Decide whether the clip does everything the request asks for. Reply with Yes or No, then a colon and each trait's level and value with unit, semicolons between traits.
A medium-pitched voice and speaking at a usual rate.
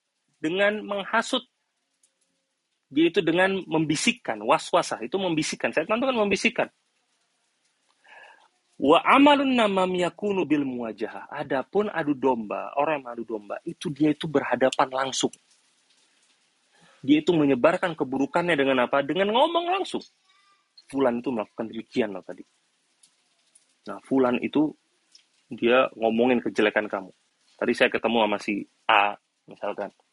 Yes: medium, 155 Hz; average, 115 wpm